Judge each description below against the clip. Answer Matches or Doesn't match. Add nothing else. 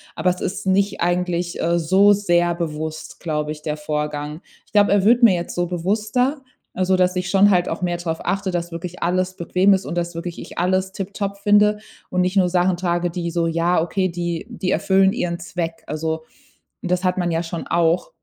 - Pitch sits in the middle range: Matches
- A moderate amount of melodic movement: Doesn't match